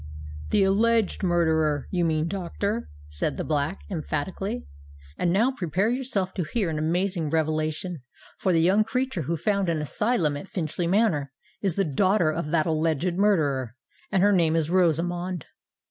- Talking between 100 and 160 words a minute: Yes, average, 155 wpm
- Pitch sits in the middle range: Yes, medium, 175 Hz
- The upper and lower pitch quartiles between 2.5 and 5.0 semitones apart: Yes, average, 4.1 semitones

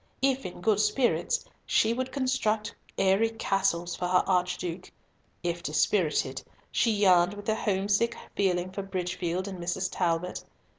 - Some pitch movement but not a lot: Yes, average, 3.2 semitones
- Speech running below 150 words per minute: Yes, average, 140 wpm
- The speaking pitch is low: No, high, 190 Hz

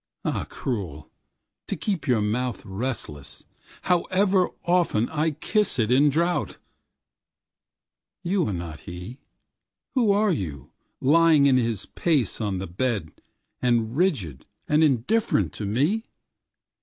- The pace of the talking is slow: Yes, slow, 105 wpm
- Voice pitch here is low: Yes, low, 130 Hz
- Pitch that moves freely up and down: Yes, wide, 8.6 semitones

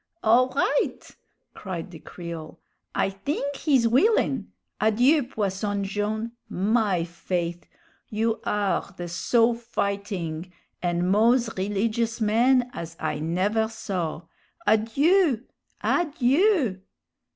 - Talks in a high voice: Yes, high, 215 Hz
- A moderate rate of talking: No, slow, 100 wpm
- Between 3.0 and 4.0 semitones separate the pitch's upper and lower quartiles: No, average, 4.5 semitones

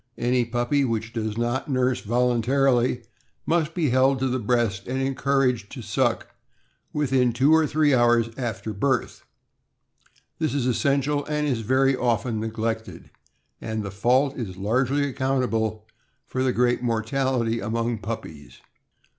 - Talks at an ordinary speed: No, slow, 130 wpm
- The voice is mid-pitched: No, low, 125 Hz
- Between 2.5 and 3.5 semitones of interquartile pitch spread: Yes, average, 3.0 semitones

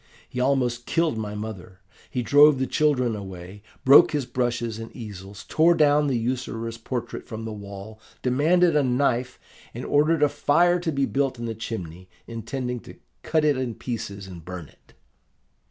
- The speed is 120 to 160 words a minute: No, average, 170 wpm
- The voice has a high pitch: No, low, 125 Hz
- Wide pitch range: No, average, 4.6 semitones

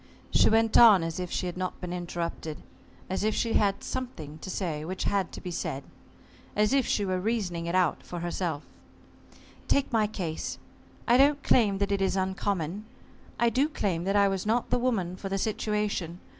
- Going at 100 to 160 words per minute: No, average, 195 wpm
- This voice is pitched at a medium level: No, high, 195 Hz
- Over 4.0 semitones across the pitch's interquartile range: No, average, 3.7 semitones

